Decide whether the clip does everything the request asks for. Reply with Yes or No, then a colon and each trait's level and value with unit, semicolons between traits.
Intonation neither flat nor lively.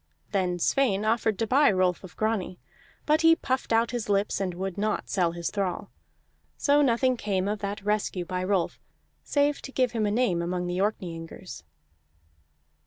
Yes: average, 4.2 semitones